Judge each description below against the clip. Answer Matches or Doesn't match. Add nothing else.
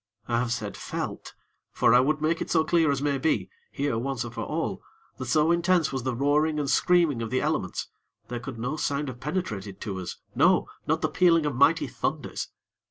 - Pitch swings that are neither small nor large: Matches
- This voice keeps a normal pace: Doesn't match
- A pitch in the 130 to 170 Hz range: Matches